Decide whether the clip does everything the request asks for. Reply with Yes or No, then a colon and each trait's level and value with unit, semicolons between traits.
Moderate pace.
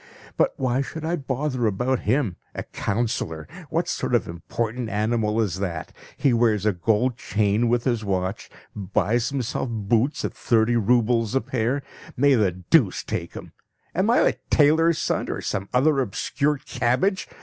Yes: average, 160 wpm